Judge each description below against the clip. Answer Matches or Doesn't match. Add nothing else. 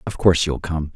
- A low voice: Matches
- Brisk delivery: Matches